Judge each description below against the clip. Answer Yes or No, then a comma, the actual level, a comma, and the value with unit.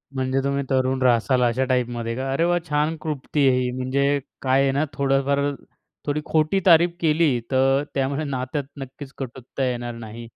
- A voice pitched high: No, low, 135 Hz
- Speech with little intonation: Yes, narrow, 2.1 semitones